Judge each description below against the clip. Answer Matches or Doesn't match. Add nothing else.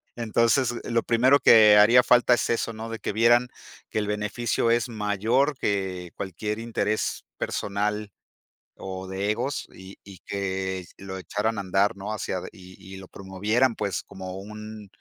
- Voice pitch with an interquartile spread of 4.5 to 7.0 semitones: Doesn't match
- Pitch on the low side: Matches